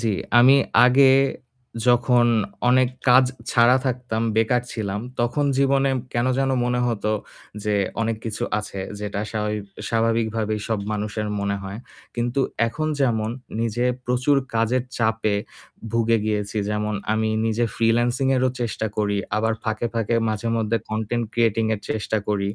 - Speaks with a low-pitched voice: Yes, low, 115 Hz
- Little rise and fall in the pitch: Yes, narrow, 2.2 semitones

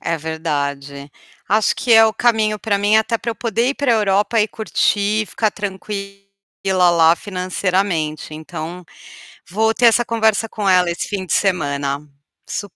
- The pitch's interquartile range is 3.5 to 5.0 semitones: Yes, average, 4.6 semitones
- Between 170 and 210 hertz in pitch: Yes, high, 200 Hz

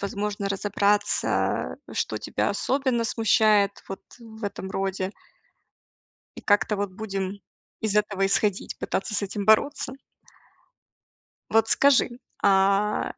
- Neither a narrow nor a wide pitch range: No, narrow, 1.9 semitones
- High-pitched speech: Yes, high, 205 Hz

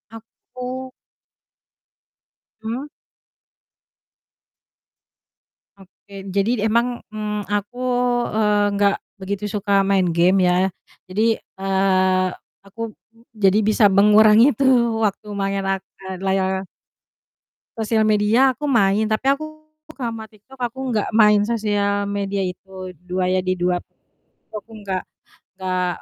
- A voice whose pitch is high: Yes, high, 205 Hz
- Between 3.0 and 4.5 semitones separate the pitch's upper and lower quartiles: No, narrow, 2.6 semitones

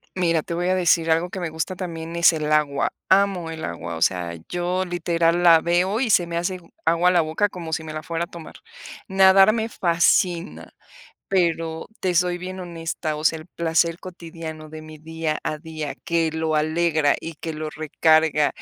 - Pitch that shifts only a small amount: Yes, narrow, 2.0 semitones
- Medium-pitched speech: Yes, medium, 165 Hz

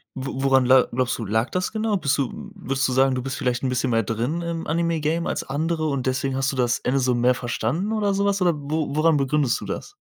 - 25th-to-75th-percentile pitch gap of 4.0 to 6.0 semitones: Yes, average, 4.4 semitones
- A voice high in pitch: No, low, 135 Hz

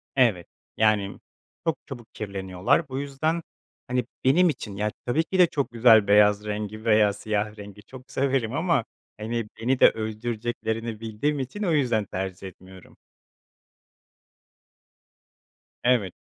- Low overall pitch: Yes, low, 115 Hz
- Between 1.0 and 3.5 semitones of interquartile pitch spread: No, average, 4.1 semitones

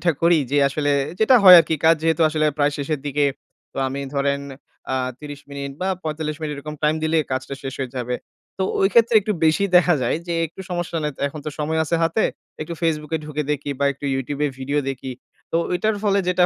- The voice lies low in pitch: No, medium, 150 Hz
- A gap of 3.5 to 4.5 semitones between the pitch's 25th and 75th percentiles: No, average, 3.1 semitones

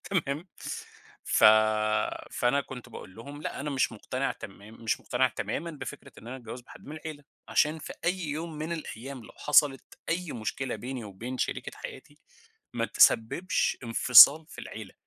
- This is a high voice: No, low, 135 Hz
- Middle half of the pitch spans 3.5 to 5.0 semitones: Yes, average, 4.2 semitones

